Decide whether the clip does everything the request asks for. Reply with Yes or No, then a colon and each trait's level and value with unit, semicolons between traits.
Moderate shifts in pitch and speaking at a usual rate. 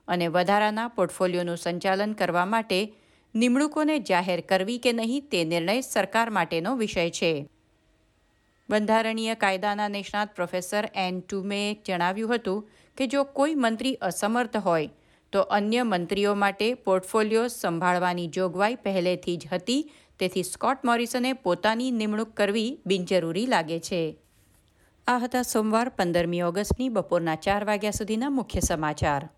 Yes: average, 4.2 semitones; average, 125 wpm